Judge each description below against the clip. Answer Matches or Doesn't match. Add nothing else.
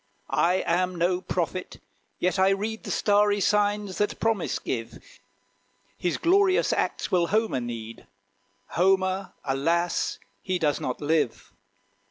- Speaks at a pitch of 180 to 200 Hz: Matches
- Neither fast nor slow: Doesn't match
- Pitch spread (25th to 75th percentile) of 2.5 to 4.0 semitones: Matches